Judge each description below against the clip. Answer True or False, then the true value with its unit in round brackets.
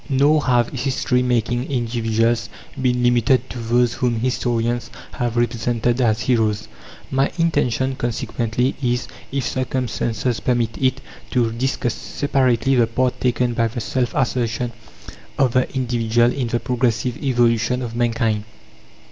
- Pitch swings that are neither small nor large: False (1.7 semitones)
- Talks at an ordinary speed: False (130 wpm)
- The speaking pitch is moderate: False (120 Hz)